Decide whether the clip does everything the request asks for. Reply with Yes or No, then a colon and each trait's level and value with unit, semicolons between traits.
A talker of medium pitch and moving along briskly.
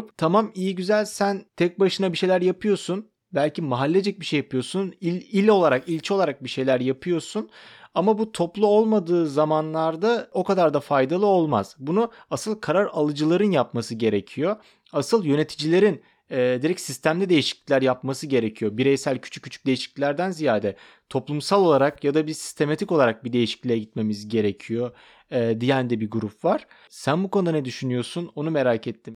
Yes: medium, 155 Hz; fast, 155 wpm